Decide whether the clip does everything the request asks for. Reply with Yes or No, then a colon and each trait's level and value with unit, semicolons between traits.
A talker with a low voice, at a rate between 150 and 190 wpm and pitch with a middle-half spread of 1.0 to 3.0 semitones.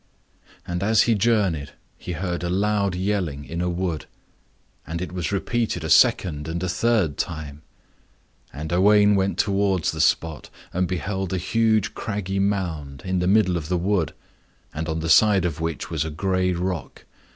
No: very low, 90 Hz; average, 170 wpm; average, 3.4 semitones